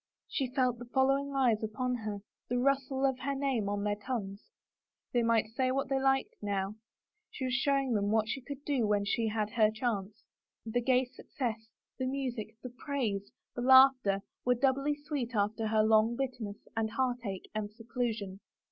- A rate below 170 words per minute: No, average, 180 wpm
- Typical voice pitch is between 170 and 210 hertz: No, high, 240 Hz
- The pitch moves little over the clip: No, average, 3.6 semitones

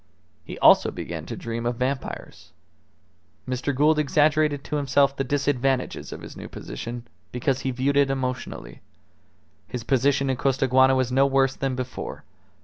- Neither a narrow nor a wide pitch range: No, narrow, 1.7 semitones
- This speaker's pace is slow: No, average, 150 wpm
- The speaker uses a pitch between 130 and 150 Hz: Yes, low, 135 Hz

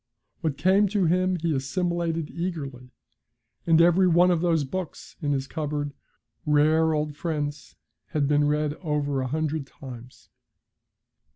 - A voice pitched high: No, medium, 155 Hz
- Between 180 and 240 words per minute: No, slow, 135 wpm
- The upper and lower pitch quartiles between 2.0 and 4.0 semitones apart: Yes, average, 2.9 semitones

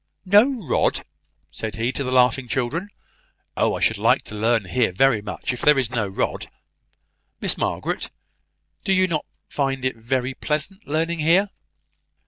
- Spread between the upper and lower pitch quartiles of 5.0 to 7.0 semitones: Yes, wide, 5.6 semitones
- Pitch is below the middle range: Yes, low, 130 Hz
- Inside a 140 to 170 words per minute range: Yes, average, 160 wpm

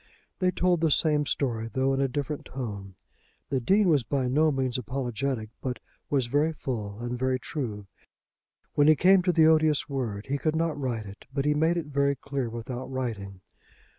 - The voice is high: No, low, 135 Hz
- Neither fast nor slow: Yes, average, 190 wpm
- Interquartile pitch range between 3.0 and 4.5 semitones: Yes, average, 3.9 semitones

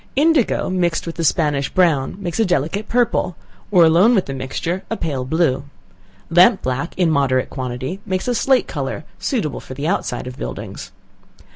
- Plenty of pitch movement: Yes, wide, 5.7 semitones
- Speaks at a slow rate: No, average, 170 wpm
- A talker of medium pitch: Yes, medium, 165 Hz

